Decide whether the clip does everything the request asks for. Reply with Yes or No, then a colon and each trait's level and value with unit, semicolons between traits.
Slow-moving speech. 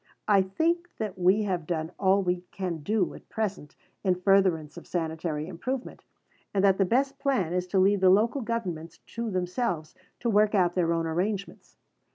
No: average, 180 wpm